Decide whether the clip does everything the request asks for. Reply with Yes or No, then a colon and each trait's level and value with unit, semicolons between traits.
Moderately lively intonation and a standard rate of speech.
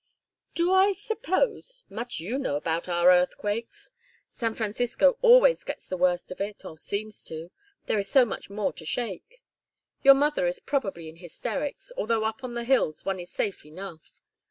No: wide, 7.6 semitones; average, 175 wpm